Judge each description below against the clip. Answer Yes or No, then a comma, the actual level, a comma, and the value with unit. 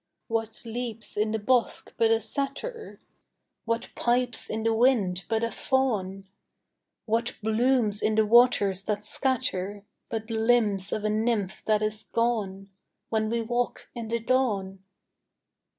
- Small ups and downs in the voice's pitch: Yes, narrow, 2.3 semitones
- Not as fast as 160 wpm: Yes, average, 140 wpm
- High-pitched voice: Yes, high, 225 Hz